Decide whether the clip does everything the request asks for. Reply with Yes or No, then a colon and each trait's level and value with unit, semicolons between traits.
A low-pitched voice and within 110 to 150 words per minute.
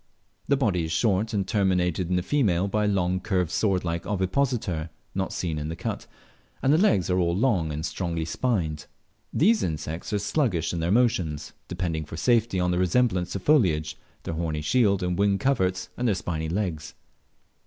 No: very low, 90 Hz; average, 185 wpm